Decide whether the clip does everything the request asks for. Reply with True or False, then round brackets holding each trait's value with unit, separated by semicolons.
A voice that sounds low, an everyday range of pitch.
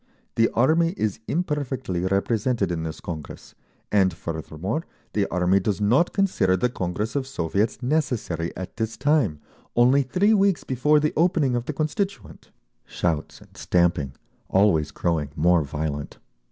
False (105 Hz; 8.5 semitones)